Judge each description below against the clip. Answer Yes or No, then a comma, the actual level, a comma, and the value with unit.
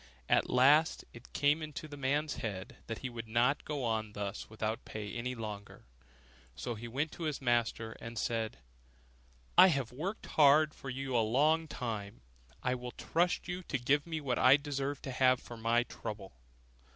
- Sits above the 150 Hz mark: No, low, 125 Hz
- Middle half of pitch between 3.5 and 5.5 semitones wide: Yes, average, 4.4 semitones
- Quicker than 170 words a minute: Yes, average, 185 wpm